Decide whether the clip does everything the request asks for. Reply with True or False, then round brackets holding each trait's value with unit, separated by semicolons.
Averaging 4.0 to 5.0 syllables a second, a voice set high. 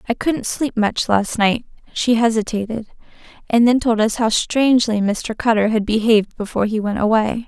False (5.4 syllables/s; 225 Hz)